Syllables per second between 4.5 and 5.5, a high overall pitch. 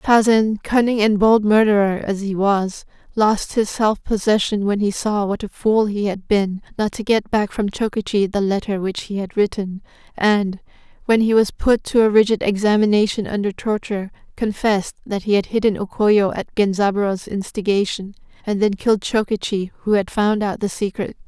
Yes: 5.0 syllables/s; high, 205 Hz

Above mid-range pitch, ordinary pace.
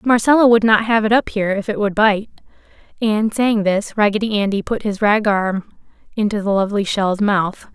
Yes: high, 210 Hz; average, 195 wpm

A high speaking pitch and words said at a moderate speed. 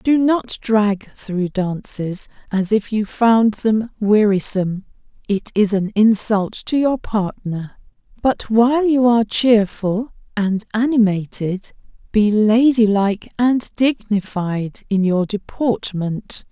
No: high, 215 Hz; slow, 120 wpm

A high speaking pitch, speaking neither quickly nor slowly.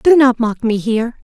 No: high, 240 Hz; fast, 230 wpm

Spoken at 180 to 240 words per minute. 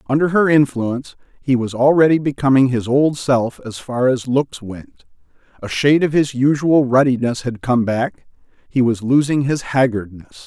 No: average, 165 wpm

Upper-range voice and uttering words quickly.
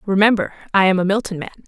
Yes: high, 195 Hz; fast, 215 wpm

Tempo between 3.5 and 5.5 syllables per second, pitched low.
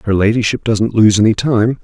Yes: 5.4 syllables/s; low, 110 Hz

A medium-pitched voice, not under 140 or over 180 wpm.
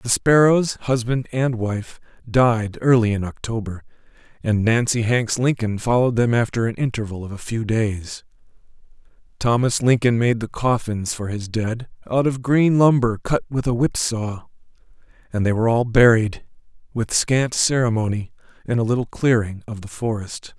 No: low, 115 Hz; average, 155 wpm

